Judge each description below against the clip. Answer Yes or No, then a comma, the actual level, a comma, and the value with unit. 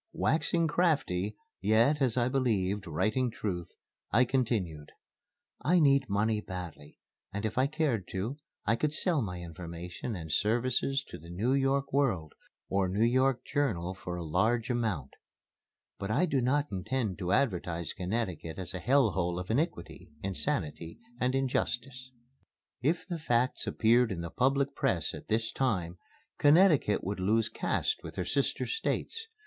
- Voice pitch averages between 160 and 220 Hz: No, low, 115 Hz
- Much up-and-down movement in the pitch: Yes, wide, 6.7 semitones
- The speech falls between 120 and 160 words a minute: Yes, average, 155 wpm